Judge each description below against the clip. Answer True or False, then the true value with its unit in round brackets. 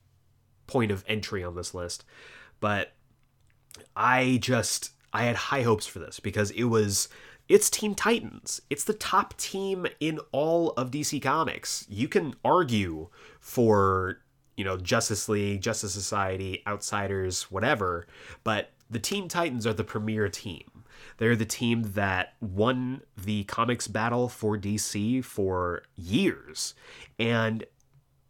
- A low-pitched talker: True (110 Hz)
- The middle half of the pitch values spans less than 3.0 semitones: False (3.7 semitones)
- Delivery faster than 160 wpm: False (135 wpm)